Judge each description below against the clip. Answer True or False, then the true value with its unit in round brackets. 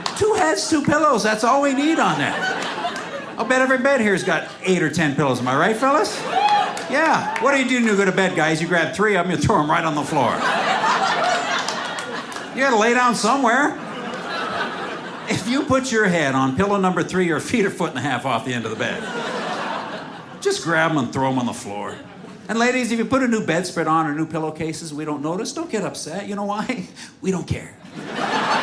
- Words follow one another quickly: True (225 wpm)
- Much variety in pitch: True (8.1 semitones)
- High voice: True (205 Hz)